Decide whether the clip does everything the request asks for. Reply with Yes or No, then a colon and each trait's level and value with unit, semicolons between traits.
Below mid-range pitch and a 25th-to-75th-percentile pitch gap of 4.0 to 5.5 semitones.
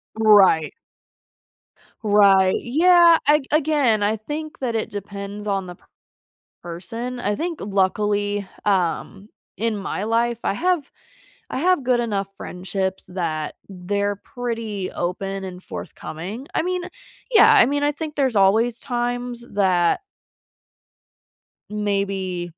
No: high, 210 Hz; average, 4.5 semitones